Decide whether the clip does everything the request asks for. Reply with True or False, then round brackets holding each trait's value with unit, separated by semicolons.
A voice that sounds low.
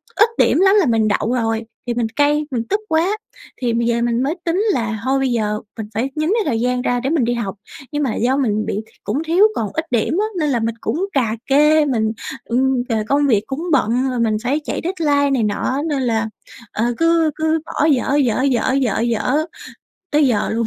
False (260 Hz)